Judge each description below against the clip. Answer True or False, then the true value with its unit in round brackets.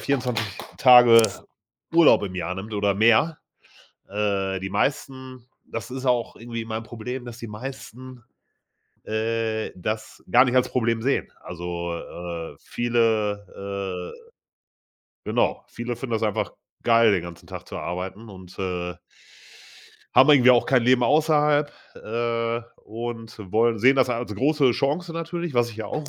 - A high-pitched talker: False (115 Hz)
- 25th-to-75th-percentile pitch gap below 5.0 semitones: True (3.8 semitones)